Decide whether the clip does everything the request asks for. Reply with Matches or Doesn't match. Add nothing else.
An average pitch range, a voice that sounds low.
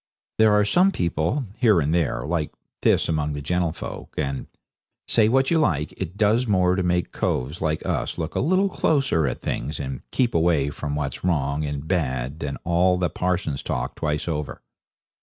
Matches